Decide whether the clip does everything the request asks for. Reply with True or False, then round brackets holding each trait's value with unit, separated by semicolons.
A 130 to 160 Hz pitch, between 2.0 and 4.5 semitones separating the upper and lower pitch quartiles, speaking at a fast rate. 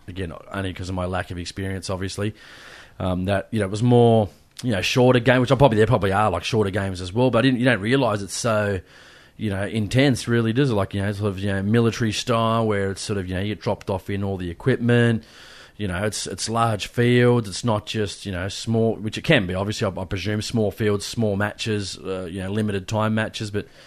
False (105 Hz; 2.8 semitones; 245 wpm)